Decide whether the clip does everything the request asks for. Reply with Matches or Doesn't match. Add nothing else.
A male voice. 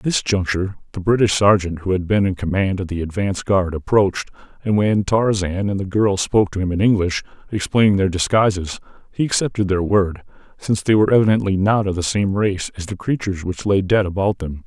Matches